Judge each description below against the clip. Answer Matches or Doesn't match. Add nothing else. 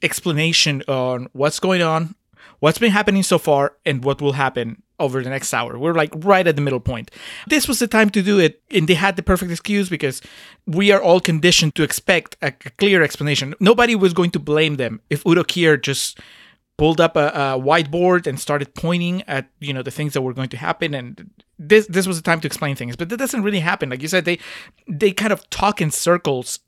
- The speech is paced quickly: Matches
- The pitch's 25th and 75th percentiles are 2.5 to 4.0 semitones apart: Doesn't match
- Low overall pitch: Doesn't match